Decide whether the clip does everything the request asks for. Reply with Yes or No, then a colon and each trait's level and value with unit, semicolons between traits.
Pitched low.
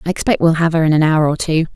No: medium, 160 Hz